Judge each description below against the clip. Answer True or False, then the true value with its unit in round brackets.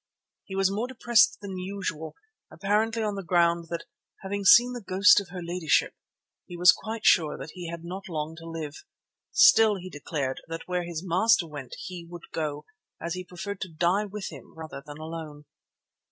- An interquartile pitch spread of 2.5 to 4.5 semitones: True (3.5 semitones)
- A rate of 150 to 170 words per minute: False (180 wpm)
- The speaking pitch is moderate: True (175 Hz)